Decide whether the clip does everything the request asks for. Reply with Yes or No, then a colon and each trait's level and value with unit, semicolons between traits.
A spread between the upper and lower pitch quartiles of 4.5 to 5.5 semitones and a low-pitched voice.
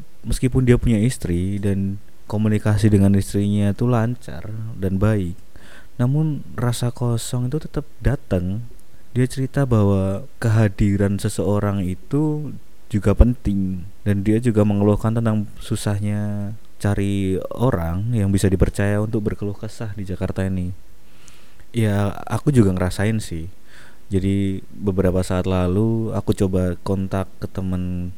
No: average, 2.8 semitones; low, 105 Hz